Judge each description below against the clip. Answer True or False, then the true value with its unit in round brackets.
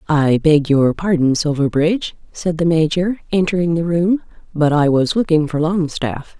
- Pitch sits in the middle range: True (160 Hz)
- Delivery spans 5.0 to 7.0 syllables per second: False (4.6 syllables/s)